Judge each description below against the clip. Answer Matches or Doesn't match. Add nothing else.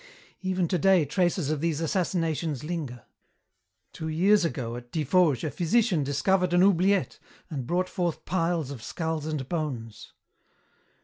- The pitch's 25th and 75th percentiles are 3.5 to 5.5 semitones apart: Matches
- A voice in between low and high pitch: Matches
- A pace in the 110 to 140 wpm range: Matches